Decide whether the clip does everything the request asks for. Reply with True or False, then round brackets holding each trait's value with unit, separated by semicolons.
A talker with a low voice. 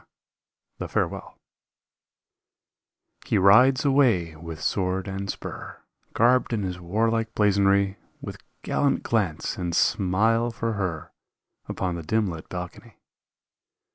True (100 Hz)